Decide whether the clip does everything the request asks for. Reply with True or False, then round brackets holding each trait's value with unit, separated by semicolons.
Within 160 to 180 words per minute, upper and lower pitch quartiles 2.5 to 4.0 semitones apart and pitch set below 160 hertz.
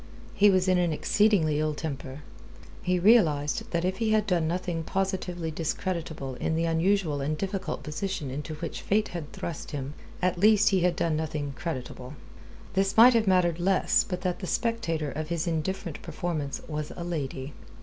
False (175 wpm; 3.7 semitones; 170 Hz)